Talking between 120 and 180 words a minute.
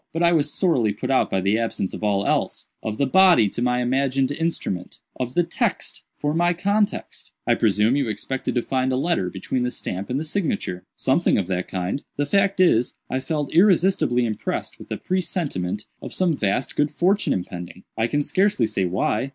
No: average, 190 wpm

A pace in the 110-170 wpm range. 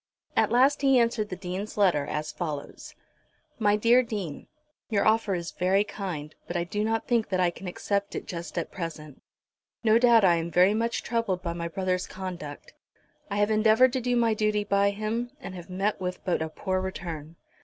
No: average, 195 wpm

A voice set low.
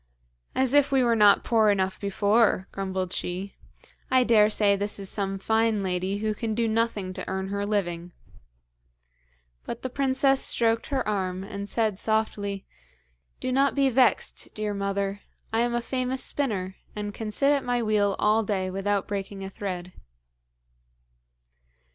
No: high, 210 Hz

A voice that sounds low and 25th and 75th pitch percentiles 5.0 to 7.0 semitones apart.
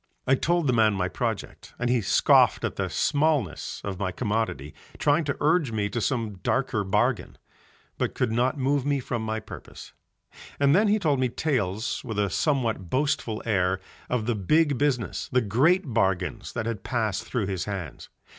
Yes: low, 115 Hz; wide, 5.4 semitones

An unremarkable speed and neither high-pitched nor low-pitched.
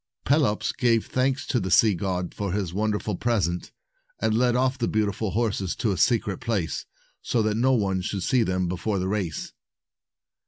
No: average, 175 wpm; low, 105 Hz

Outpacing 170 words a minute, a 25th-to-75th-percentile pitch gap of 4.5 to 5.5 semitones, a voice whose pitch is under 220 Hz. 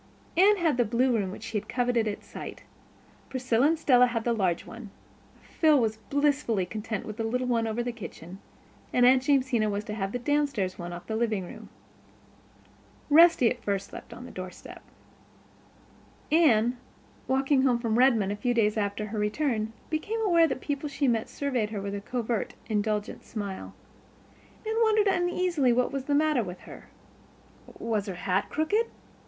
No: average, 180 wpm; average, 5.0 semitones; high, 240 Hz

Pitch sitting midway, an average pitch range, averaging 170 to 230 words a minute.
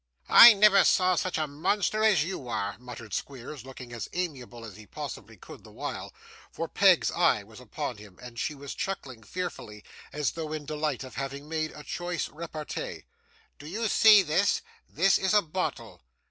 No: medium, 150 Hz; wide, 6.7 semitones; average, 180 wpm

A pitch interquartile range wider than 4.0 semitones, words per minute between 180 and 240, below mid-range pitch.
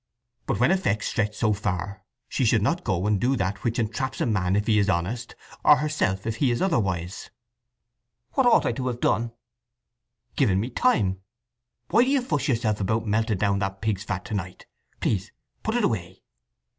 Yes: average, 4.5 semitones; average, 190 wpm; low, 110 Hz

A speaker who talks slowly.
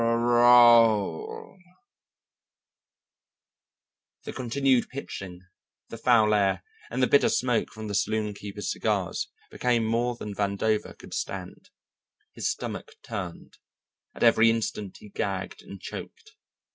Yes: slow, 110 wpm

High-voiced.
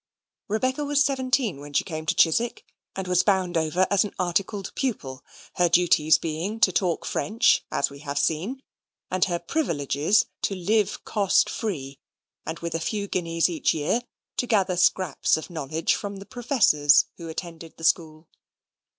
No: medium, 180 Hz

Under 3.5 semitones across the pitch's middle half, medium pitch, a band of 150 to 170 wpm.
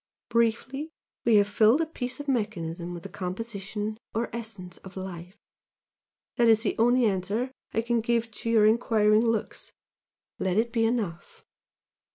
No: average, 3.0 semitones; high, 220 Hz; average, 155 wpm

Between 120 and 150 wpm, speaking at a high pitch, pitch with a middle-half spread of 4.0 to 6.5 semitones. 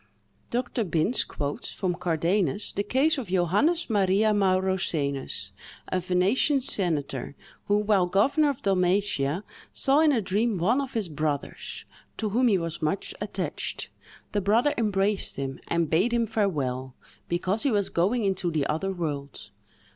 Yes: average, 145 wpm; high, 195 Hz; average, 4.8 semitones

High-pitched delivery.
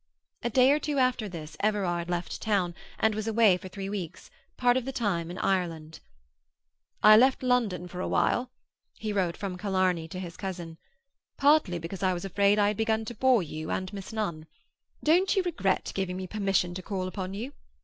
Yes: high, 195 Hz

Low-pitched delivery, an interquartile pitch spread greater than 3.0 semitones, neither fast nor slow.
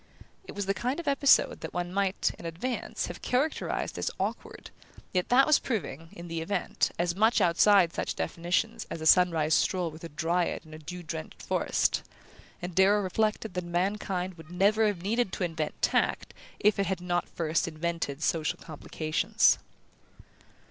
No: medium, 180 Hz; average, 3.6 semitones; average, 170 wpm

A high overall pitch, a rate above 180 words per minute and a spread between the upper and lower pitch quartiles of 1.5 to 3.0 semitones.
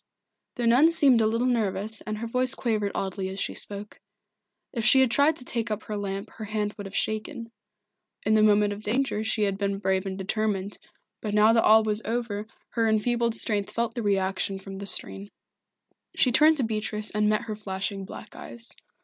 Yes: high, 215 Hz; average, 200 wpm; narrow, 2.5 semitones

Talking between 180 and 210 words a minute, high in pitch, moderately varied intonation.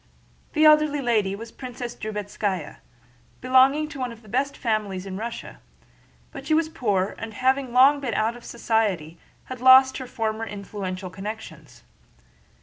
No: average, 155 wpm; high, 235 Hz; average, 4.1 semitones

